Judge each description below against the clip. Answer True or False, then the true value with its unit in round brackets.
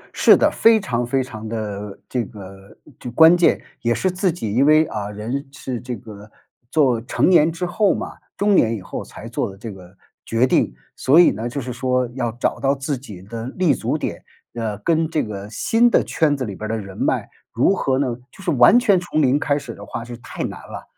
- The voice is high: False (125 Hz)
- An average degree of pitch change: False (6.0 semitones)